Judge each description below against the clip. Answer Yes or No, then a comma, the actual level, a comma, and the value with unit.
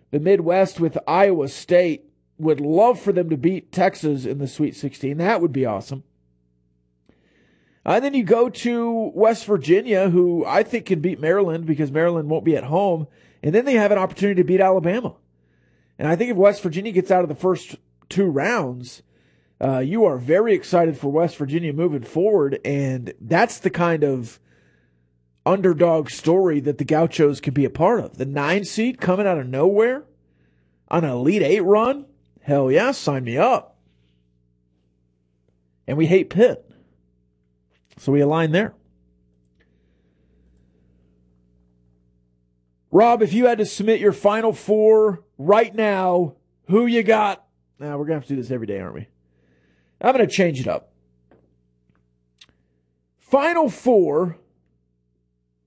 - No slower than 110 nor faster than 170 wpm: Yes, average, 155 wpm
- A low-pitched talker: No, medium, 145 Hz